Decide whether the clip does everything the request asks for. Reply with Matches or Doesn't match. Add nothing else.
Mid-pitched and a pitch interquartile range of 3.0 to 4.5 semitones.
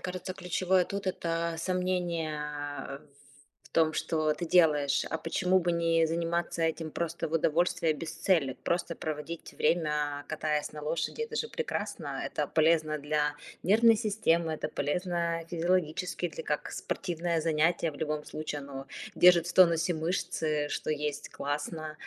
Doesn't match